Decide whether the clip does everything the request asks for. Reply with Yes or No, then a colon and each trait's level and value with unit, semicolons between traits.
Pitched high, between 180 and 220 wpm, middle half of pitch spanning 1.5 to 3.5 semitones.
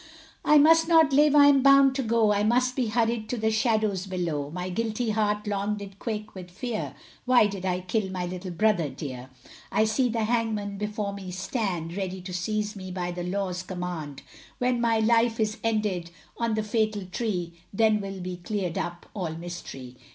No: high, 210 Hz; average, 190 wpm; average, 4.0 semitones